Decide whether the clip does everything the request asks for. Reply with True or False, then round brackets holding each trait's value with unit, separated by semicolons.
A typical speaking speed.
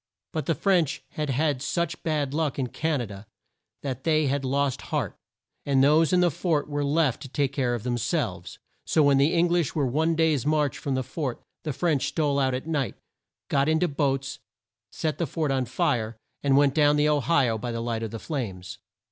False (220 wpm)